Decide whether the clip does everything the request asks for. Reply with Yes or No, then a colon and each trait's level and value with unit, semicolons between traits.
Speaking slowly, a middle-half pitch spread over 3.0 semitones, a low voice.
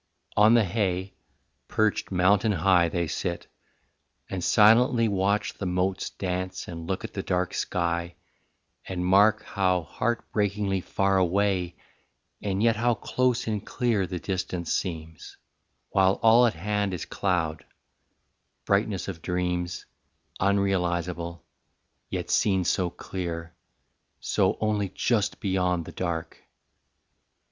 No: slow, 120 wpm; narrow, 2.6 semitones; very low, 95 Hz